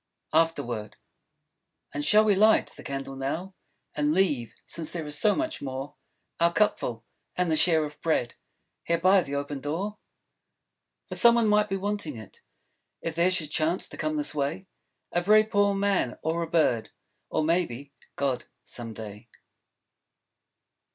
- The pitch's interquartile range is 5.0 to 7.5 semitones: Yes, wide, 5.5 semitones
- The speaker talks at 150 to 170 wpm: Yes, average, 160 wpm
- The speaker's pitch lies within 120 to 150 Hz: No, medium, 160 Hz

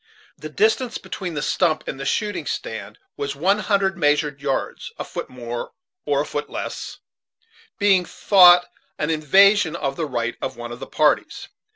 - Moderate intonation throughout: No, wide, 5.8 semitones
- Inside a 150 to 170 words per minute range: Yes, average, 165 wpm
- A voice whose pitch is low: No, medium, 155 Hz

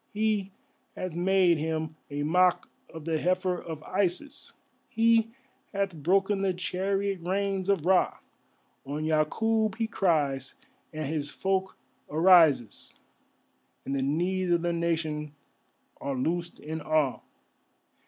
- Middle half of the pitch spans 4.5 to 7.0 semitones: No, average, 3.7 semitones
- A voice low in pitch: No, medium, 175 Hz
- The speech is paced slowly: Yes, slow, 125 wpm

